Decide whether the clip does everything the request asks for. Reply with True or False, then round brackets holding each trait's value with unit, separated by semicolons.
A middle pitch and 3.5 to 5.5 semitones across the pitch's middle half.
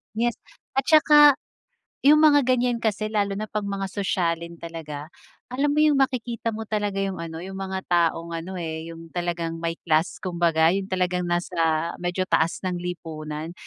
True (180 Hz; 4.3 semitones)